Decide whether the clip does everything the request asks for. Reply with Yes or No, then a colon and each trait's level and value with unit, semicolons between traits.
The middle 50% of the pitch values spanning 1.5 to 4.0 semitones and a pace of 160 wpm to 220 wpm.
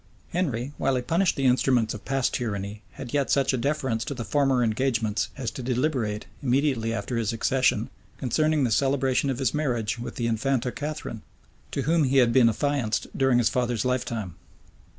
Yes: average, 3.1 semitones; average, 175 wpm